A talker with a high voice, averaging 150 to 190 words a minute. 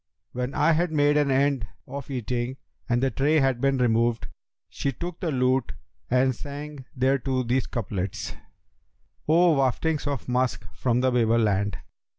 No: low, 130 Hz; average, 160 wpm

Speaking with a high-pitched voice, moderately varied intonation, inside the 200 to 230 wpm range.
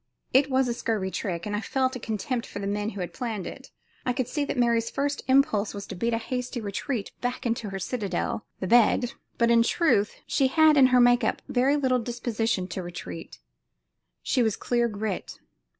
Yes: high, 235 Hz; average, 3.6 semitones; fast, 205 wpm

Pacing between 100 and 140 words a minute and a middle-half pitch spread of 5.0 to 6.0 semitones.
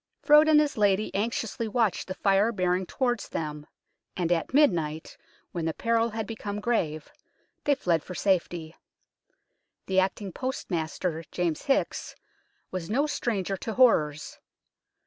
Yes: slow, 135 wpm; wide, 5.4 semitones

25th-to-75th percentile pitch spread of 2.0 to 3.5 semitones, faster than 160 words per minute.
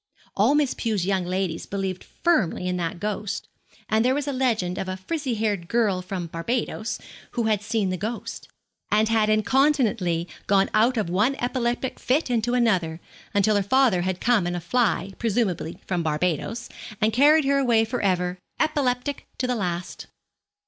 No: average, 5.0 semitones; average, 170 wpm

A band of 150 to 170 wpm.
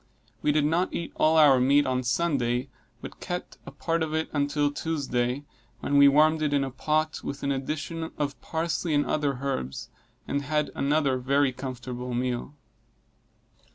Yes: average, 160 wpm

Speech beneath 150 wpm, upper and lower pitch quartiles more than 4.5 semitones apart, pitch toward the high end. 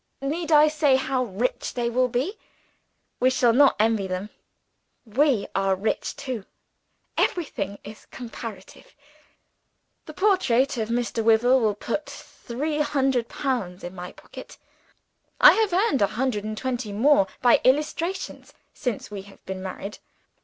Yes: average, 140 wpm; average, 5.0 semitones; high, 245 Hz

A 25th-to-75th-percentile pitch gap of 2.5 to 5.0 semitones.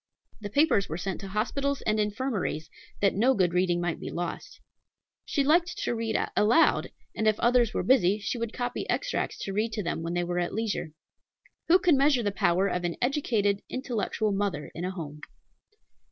No: wide, 5.6 semitones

